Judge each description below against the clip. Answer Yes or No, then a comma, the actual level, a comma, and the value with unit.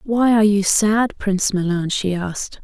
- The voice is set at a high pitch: Yes, high, 200 Hz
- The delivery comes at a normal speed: Yes, average, 180 wpm